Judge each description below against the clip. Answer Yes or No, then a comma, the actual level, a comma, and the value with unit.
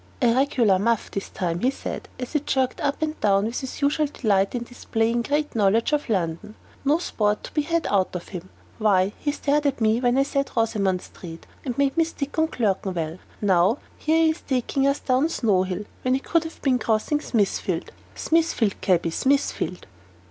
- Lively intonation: Yes, wide, 6.2 semitones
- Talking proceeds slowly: No, average, 195 wpm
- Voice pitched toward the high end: Yes, high, 240 Hz